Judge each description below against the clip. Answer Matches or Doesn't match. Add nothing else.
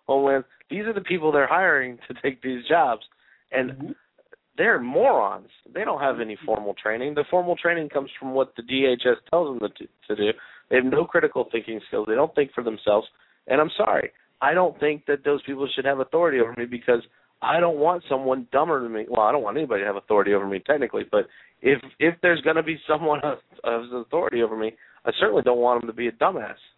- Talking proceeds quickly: Matches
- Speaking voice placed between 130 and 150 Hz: Matches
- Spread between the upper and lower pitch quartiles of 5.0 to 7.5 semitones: Matches